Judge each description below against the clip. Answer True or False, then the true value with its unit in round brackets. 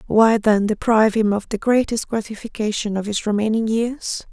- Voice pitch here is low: False (220 Hz)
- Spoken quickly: False (165 wpm)